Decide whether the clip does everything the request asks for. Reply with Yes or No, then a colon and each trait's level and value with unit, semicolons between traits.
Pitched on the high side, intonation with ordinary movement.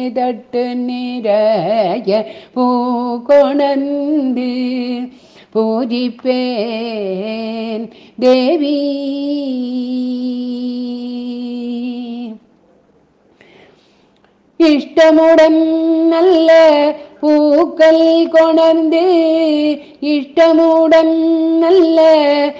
Yes: very high, 275 Hz; average, 4.6 semitones